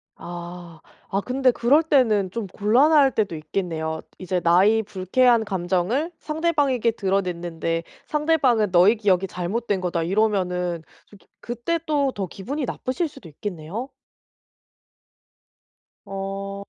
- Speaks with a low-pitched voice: No, high, 200 Hz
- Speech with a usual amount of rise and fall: No, wide, 6.0 semitones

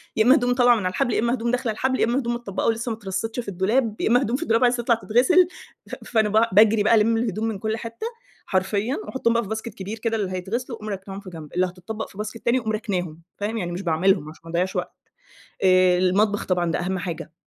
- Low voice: No, high, 220 Hz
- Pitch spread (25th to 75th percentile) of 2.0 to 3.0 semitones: No, average, 3.8 semitones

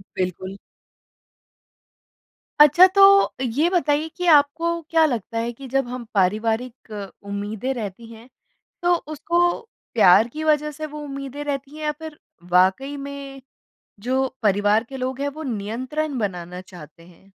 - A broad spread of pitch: Yes, wide, 6.1 semitones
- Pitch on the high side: Yes, very high, 265 Hz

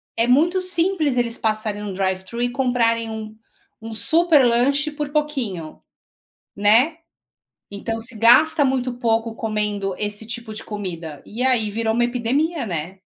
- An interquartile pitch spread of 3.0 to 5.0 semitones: Yes, average, 4.1 semitones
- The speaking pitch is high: Yes, high, 230 Hz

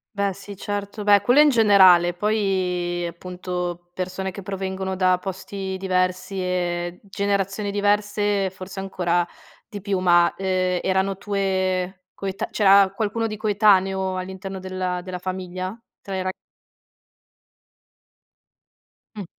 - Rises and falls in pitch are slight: Yes, narrow, 1.6 semitones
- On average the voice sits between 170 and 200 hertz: Yes, high, 190 Hz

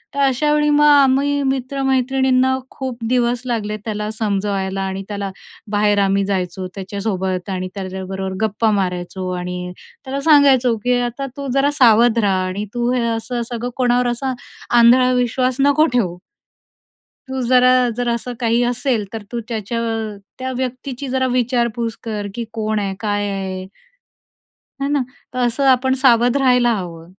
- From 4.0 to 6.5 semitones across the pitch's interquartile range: Yes, average, 4.3 semitones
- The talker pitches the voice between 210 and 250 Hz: Yes, high, 235 Hz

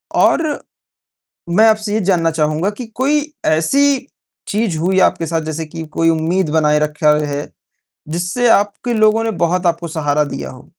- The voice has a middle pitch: Yes, medium, 170 Hz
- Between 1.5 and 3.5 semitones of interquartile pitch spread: No, wide, 5.5 semitones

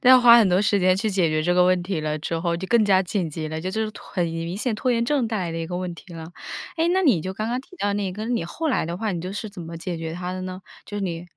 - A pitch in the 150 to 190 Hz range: Yes, medium, 185 Hz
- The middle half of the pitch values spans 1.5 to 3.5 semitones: No, average, 4.4 semitones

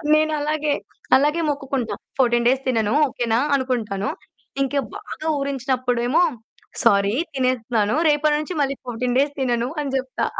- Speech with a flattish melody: No, average, 3.2 semitones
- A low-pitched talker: No, very high, 260 Hz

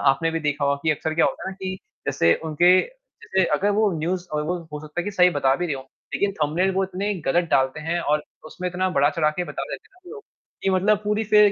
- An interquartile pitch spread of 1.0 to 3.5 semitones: No, average, 4.0 semitones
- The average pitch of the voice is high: No, medium, 175 Hz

